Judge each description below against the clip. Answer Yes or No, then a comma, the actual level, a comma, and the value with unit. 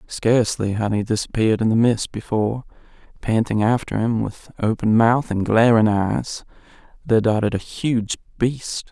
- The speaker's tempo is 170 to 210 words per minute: No, average, 150 wpm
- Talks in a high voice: No, low, 110 Hz